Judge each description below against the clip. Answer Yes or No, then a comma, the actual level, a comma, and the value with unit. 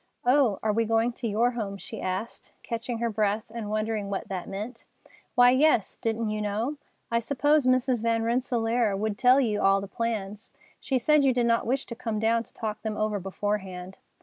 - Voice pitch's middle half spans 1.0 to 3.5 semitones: Yes, average, 2.7 semitones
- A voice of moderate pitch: No, high, 225 Hz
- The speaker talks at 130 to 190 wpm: No, average, 200 wpm